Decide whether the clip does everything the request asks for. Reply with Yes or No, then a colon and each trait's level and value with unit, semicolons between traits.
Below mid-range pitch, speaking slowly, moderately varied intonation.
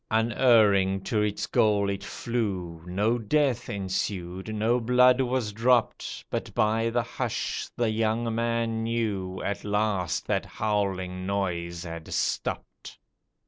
Yes: low, 105 Hz; slow, 125 wpm; average, 3.2 semitones